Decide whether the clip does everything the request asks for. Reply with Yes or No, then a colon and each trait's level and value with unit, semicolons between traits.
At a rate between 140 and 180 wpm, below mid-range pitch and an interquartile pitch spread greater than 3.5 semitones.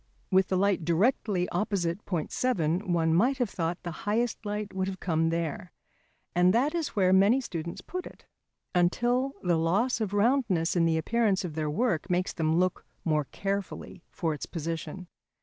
No: average, 175 wpm; medium, 185 Hz; average, 4.2 semitones